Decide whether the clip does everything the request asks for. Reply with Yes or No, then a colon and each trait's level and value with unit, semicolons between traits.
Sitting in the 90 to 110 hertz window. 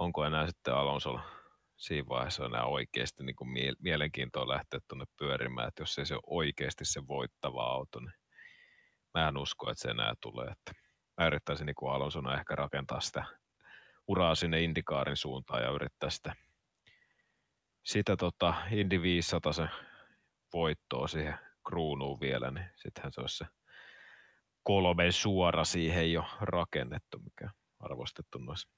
No: very low, 80 Hz